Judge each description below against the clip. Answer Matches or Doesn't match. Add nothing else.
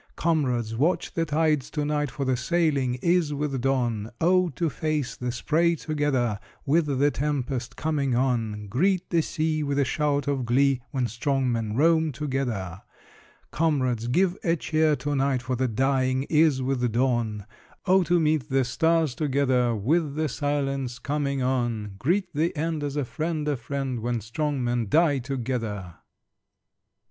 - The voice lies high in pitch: Doesn't match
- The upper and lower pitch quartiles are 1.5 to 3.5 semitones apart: Doesn't match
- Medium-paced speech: Matches